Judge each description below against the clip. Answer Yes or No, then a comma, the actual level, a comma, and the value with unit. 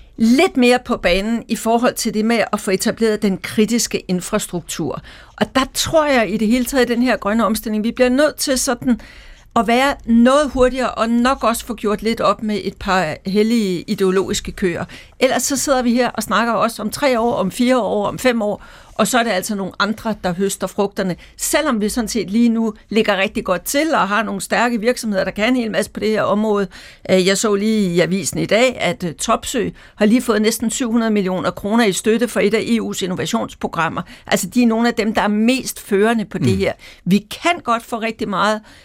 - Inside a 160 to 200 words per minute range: No, average, 220 wpm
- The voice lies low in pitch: No, high, 220 Hz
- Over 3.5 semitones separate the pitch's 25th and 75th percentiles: No, average, 3.2 semitones